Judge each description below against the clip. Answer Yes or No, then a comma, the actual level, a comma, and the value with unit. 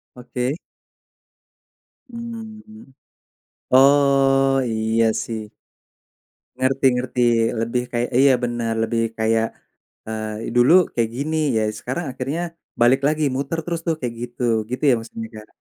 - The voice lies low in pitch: Yes, low, 125 Hz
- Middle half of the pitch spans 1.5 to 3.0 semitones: No, average, 3.6 semitones